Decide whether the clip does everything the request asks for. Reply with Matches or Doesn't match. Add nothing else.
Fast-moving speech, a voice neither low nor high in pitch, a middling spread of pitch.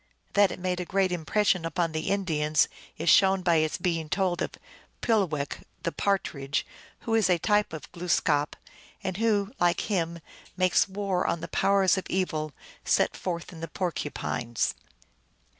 Doesn't match